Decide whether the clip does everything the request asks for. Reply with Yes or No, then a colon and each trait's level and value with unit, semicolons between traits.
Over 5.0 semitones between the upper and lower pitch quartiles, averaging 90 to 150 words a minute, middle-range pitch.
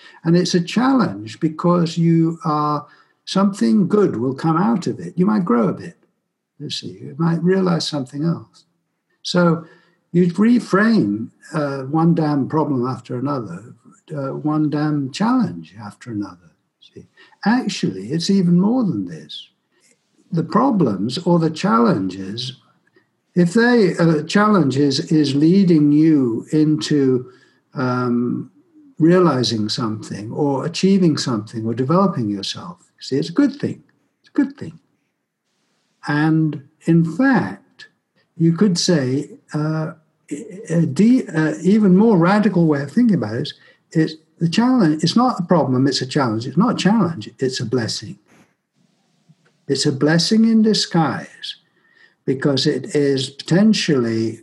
Yes: wide, 5.4 semitones; average, 140 wpm; medium, 165 Hz